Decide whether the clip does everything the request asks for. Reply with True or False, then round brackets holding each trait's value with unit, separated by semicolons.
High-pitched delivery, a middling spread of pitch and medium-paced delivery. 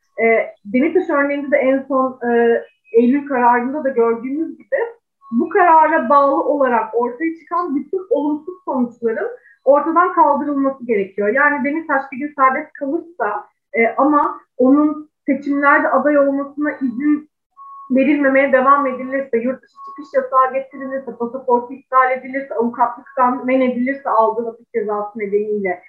True (275 Hz; 3.2 semitones; 130 wpm)